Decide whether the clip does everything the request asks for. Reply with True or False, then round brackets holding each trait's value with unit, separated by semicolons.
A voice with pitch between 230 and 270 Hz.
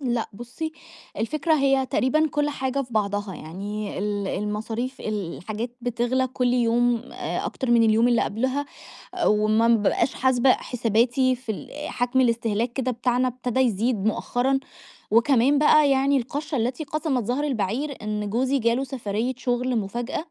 True (245 Hz)